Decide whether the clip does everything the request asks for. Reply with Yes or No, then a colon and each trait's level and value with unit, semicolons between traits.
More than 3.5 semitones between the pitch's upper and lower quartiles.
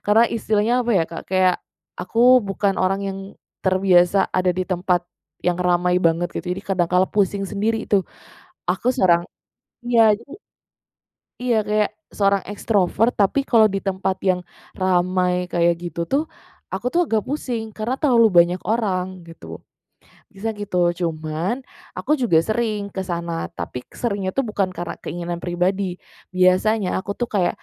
No: average, 3.2 semitones